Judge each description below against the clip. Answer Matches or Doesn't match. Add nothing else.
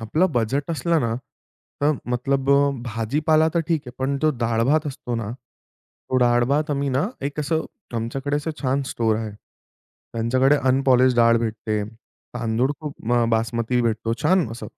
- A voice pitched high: Doesn't match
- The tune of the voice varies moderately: Matches